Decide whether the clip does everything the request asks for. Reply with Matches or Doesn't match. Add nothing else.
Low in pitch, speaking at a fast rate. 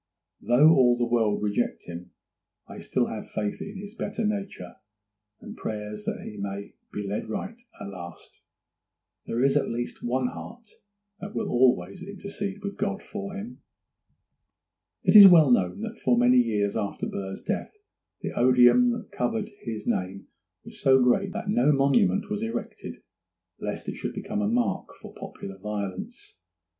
Doesn't match